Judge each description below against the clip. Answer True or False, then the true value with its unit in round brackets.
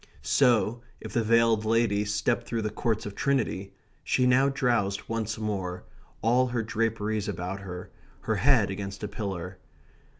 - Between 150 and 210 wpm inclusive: True (155 wpm)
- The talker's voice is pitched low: True (110 Hz)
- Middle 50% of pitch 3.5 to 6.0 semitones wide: False (2.8 semitones)